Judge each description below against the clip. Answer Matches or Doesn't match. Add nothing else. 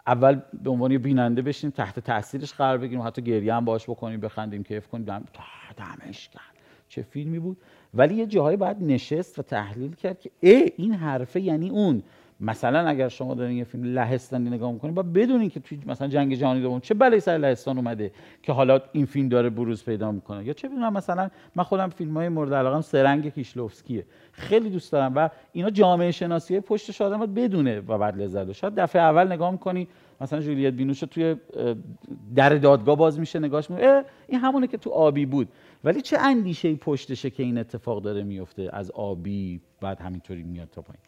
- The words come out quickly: Matches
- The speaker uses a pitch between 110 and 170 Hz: Matches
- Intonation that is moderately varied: Doesn't match